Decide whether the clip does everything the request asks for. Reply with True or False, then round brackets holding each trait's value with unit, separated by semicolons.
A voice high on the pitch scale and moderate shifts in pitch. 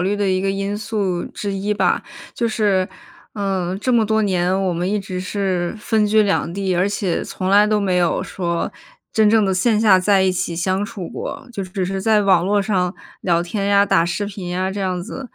False (195 Hz; 2.2 semitones)